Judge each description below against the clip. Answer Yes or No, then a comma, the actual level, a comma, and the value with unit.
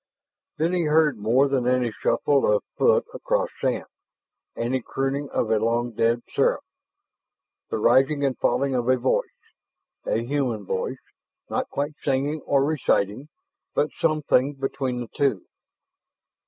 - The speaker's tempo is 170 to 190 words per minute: No, average, 140 wpm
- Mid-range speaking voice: No, low, 130 Hz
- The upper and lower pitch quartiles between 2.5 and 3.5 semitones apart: Yes, average, 3.2 semitones